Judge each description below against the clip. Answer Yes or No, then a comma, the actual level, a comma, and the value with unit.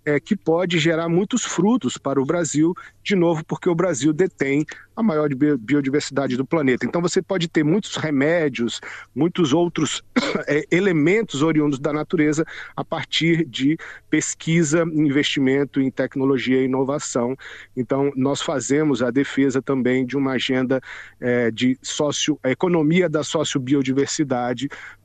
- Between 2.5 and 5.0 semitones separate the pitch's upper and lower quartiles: Yes, average, 3.7 semitones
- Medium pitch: Yes, medium, 150 Hz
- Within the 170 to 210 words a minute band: No, average, 135 wpm